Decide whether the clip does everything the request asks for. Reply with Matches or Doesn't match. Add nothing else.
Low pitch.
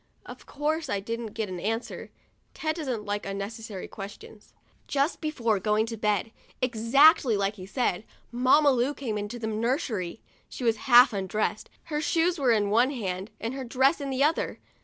Doesn't match